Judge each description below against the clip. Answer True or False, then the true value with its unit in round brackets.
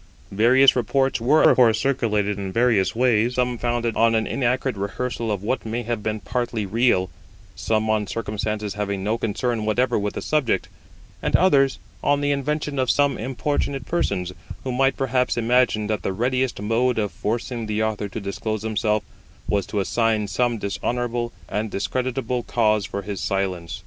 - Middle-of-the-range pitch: False (115 Hz)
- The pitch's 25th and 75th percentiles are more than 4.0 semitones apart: False (3.2 semitones)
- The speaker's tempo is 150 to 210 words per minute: True (170 wpm)